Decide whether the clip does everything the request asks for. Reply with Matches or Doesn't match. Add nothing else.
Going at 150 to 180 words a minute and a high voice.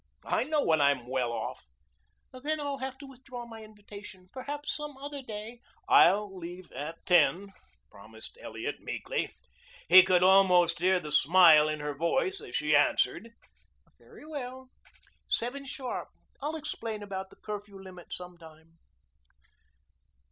Doesn't match